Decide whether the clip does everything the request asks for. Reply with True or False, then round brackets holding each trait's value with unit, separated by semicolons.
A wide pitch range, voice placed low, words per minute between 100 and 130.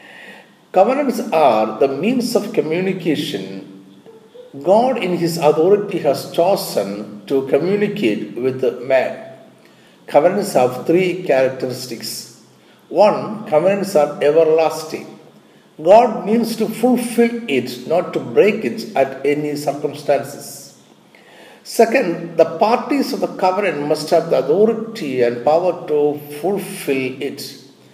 False (7.4 semitones; 170 Hz; 110 wpm)